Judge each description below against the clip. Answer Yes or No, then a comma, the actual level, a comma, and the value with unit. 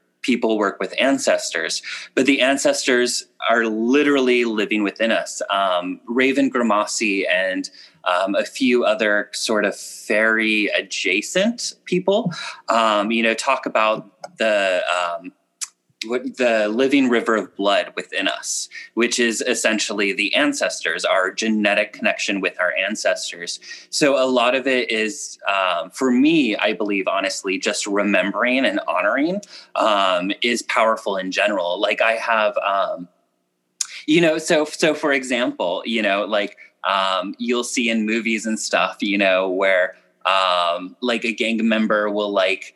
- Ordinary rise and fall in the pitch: No, wide, 5.8 semitones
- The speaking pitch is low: Yes, low, 115 Hz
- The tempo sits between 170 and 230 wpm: No, average, 140 wpm